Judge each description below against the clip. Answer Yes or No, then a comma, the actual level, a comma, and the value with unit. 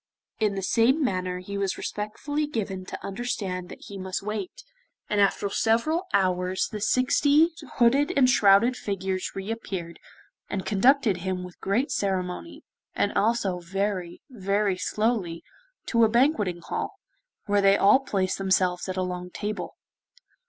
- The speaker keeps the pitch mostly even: No, average, 3.8 semitones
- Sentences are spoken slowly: No, average, 145 wpm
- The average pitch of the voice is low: No, high, 200 Hz